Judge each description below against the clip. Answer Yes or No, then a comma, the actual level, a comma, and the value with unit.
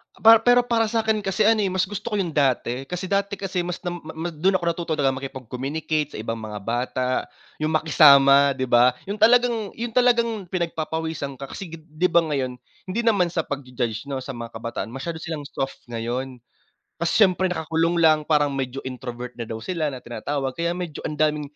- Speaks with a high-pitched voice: No, medium, 155 Hz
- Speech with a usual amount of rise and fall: No, wide, 5.9 semitones